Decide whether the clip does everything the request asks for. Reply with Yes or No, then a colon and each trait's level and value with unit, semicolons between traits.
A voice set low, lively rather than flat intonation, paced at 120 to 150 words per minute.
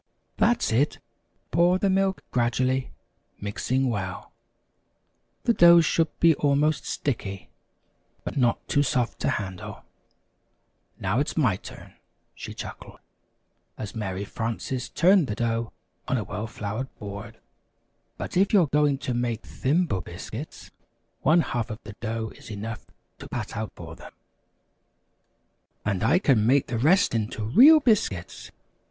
Yes: low, 125 Hz; wide, 6.2 semitones; average, 140 wpm